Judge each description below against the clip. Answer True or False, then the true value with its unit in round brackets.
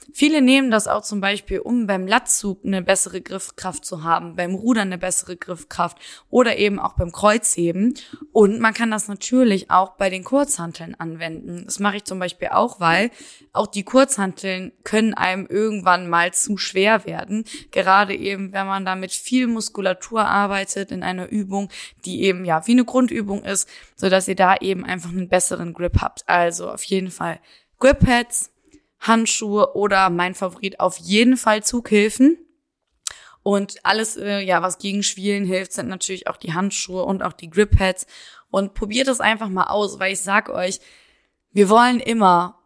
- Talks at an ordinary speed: True (175 wpm)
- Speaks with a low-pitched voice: False (200 Hz)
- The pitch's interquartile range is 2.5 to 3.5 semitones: True (3.1 semitones)